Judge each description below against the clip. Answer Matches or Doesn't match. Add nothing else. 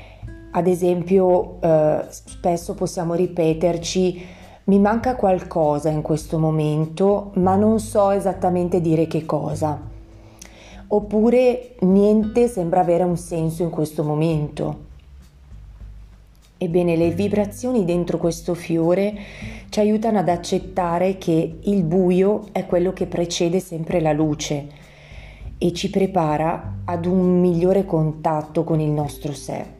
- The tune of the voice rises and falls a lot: Doesn't match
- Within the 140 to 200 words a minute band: Doesn't match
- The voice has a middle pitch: Matches